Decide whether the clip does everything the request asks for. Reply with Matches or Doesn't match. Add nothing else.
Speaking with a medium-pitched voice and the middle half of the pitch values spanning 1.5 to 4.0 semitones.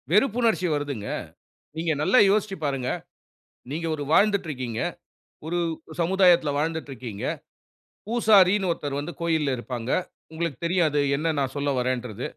Doesn't match